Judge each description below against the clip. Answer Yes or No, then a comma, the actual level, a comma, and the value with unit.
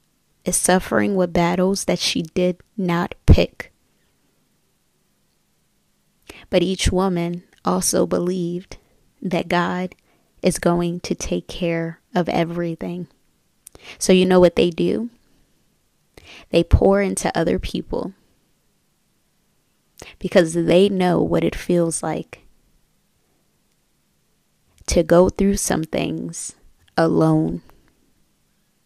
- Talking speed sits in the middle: No, slow, 100 wpm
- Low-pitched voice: No, medium, 175 Hz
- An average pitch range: No, narrow, 1.6 semitones